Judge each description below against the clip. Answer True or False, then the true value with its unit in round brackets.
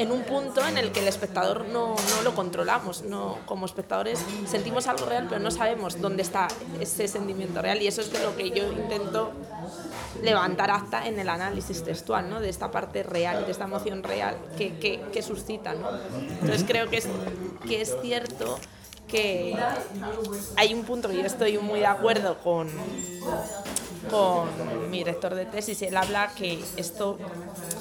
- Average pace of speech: True (175 wpm)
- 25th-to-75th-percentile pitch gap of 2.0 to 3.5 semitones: True (2.9 semitones)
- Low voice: False (205 Hz)